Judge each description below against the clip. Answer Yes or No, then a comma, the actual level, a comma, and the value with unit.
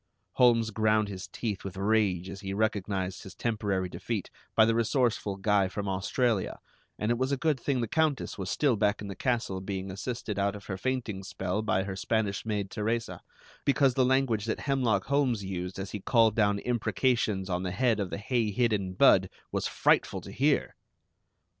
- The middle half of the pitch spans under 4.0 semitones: Yes, average, 3.5 semitones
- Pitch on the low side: Yes, low, 105 Hz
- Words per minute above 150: Yes, average, 190 wpm